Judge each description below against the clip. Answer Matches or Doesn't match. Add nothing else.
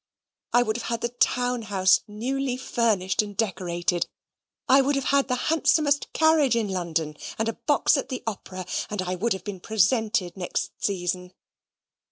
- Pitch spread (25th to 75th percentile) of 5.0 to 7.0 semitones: Matches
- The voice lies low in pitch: Doesn't match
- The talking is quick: Doesn't match